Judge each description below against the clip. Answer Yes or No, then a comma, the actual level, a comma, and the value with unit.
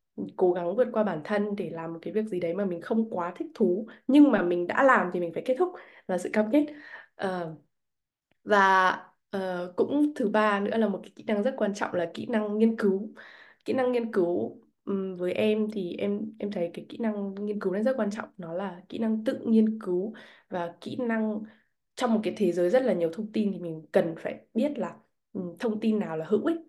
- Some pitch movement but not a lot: Yes, average, 3.8 semitones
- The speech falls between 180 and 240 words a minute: Yes, average, 235 wpm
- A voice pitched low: No, high, 210 Hz